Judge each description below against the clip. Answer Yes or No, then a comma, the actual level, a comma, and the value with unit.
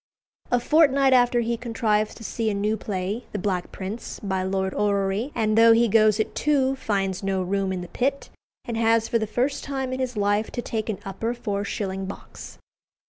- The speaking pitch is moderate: No, high, 220 Hz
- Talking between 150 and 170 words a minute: No, average, 200 wpm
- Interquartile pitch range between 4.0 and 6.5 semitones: No, average, 3.5 semitones